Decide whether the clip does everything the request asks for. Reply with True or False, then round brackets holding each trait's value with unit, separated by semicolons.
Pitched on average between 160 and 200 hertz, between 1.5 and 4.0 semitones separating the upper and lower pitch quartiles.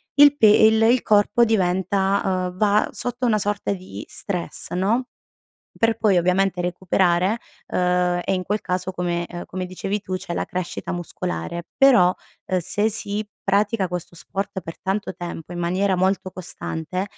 True (190 Hz; 2.6 semitones)